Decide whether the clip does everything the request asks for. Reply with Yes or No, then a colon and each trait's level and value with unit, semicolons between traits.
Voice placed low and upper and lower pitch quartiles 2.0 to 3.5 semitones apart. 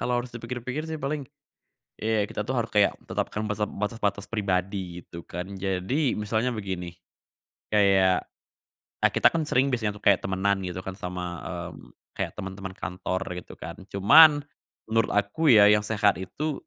No: low, 105 Hz; average, 4.1 semitones